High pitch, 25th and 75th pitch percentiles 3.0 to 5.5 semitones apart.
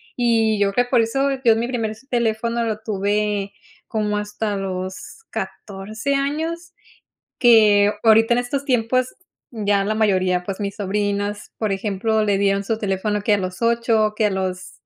No: high, 215 Hz; narrow, 2.5 semitones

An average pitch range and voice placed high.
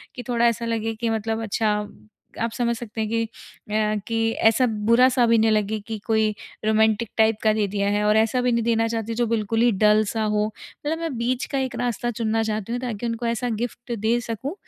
No: narrow, 1.5 semitones; high, 225 Hz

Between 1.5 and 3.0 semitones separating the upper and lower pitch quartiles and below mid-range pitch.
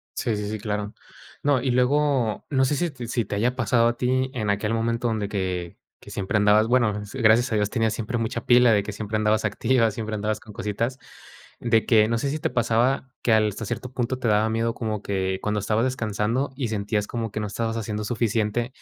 Yes: narrow, 2.5 semitones; low, 110 Hz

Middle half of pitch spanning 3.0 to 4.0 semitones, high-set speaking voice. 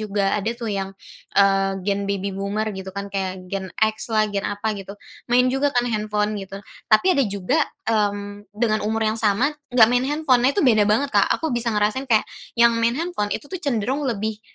Yes: average, 3.5 semitones; high, 215 Hz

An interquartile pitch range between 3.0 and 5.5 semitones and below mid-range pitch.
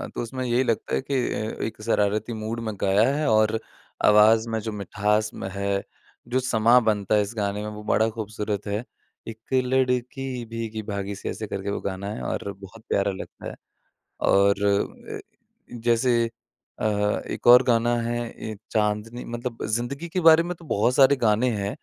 No: narrow, 2.6 semitones; low, 110 Hz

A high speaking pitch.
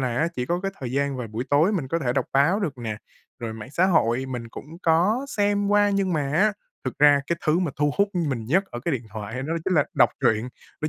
No: medium, 145 Hz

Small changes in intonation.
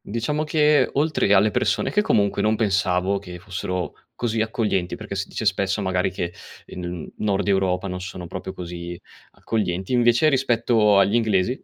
No: average, 3.8 semitones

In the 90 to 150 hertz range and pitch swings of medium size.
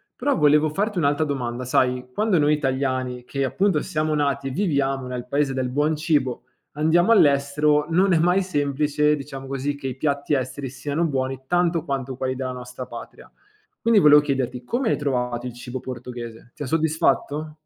Yes: medium, 140 Hz; average, 3.0 semitones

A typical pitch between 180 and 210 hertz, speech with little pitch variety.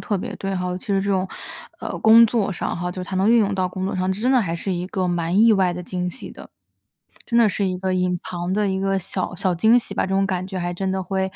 Yes: high, 190 Hz; narrow, 1.7 semitones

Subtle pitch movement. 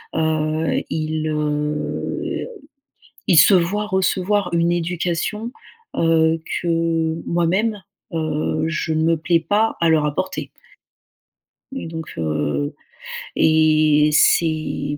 Yes: narrow, 2.0 semitones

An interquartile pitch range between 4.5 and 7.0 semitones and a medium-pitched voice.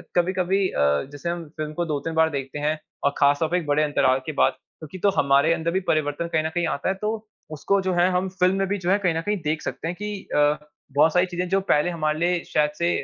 No: average, 3.3 semitones; medium, 165 Hz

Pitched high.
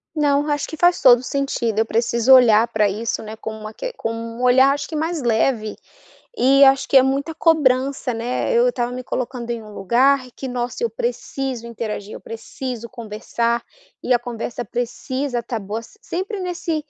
Yes: very high, 250 Hz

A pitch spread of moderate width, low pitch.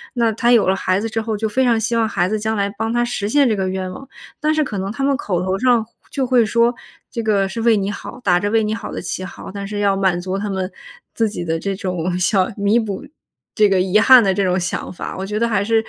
No: average, 3.3 semitones; high, 210 Hz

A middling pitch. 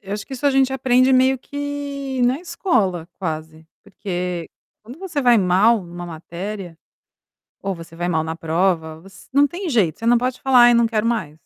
No: high, 215 Hz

